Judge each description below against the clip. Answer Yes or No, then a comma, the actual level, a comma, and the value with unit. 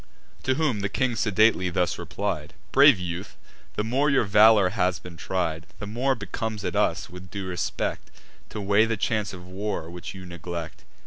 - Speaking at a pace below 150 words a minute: No, average, 180 wpm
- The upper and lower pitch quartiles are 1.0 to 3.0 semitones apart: No, average, 3.8 semitones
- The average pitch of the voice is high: No, low, 100 Hz